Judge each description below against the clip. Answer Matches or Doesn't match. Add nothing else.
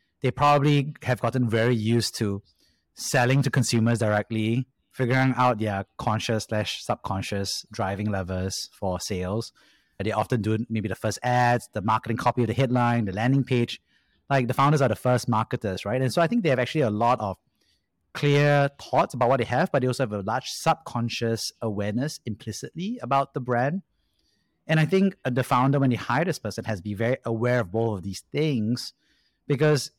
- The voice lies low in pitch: Matches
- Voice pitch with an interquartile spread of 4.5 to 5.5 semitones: Doesn't match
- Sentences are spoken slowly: Doesn't match